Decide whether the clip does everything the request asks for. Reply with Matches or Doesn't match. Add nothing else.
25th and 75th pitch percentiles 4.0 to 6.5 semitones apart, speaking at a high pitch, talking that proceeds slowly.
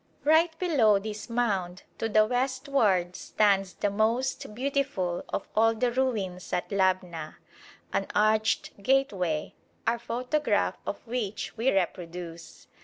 Matches